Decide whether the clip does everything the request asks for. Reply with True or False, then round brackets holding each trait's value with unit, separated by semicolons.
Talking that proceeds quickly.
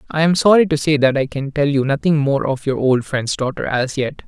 True (265 wpm)